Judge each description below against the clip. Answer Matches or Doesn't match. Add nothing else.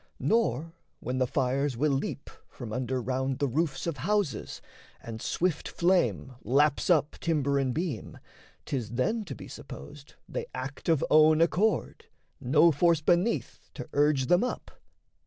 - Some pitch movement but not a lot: Matches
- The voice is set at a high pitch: Doesn't match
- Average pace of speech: Matches